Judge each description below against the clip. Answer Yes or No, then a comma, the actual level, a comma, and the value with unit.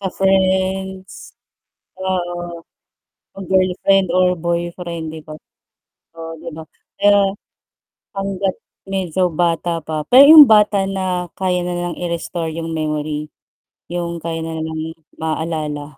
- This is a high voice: No, medium, 175 Hz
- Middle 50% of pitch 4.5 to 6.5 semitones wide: No, narrow, 2.5 semitones